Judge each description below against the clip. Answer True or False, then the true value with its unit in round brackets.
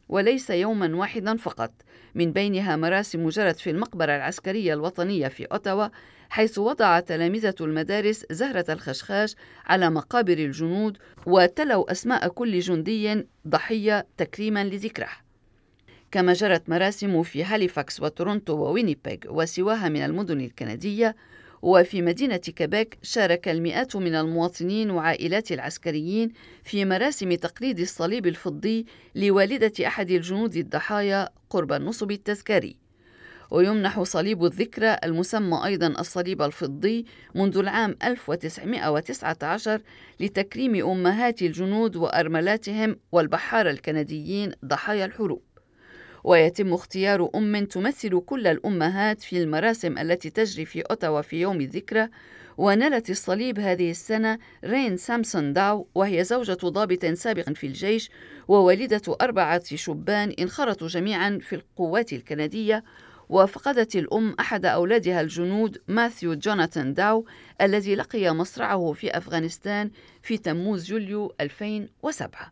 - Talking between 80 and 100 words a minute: False (110 wpm)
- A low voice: False (190 Hz)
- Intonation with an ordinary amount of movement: True (4.1 semitones)